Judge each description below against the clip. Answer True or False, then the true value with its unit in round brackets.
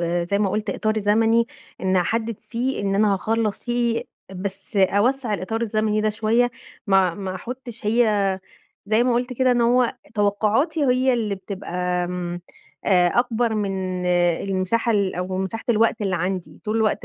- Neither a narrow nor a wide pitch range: True (3.4 semitones)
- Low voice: False (210 Hz)